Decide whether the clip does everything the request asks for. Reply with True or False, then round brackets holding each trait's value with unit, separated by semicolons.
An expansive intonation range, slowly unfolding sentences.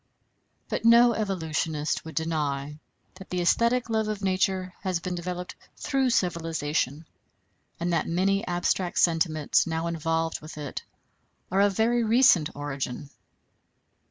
False (3.8 semitones; 130 wpm)